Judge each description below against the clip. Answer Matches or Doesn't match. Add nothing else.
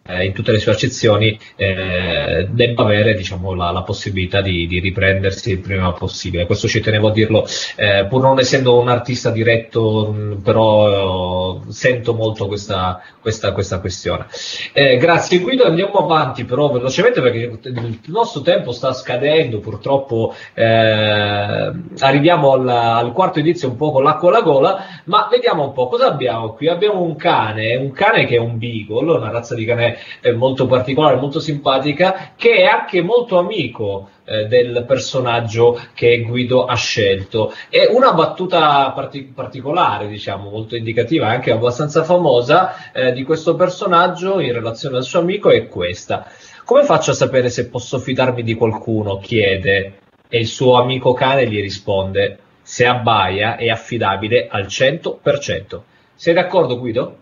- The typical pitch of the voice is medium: Doesn't match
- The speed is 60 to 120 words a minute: Doesn't match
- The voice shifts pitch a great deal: Matches